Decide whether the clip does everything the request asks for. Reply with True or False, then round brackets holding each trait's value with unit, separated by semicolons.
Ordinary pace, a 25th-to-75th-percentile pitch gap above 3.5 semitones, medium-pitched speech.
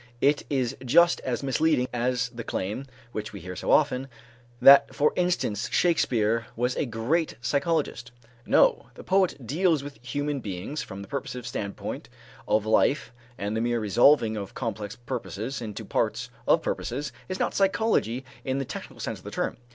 False (165 wpm; 4.4 semitones; 125 Hz)